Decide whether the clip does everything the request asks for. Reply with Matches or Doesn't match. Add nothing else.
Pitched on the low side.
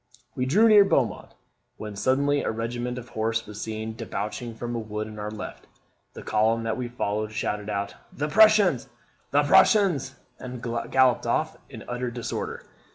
Matches